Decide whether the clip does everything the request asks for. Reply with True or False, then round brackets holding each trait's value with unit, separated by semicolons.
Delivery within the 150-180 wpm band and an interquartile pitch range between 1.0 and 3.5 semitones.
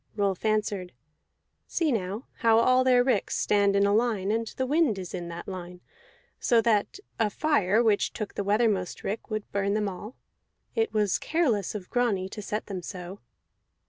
True (175 wpm; 3.2 semitones)